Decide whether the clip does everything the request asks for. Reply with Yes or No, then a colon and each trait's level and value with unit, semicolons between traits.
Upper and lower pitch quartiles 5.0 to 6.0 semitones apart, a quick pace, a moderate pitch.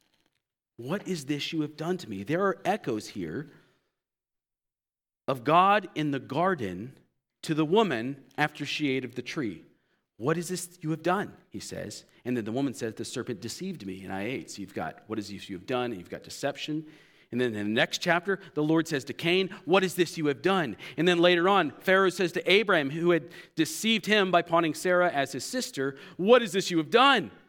Yes: average, 5.3 semitones; fast, 220 wpm; medium, 160 Hz